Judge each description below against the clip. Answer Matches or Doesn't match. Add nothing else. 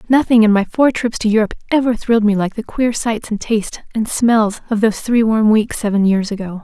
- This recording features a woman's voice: Matches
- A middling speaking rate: Doesn't match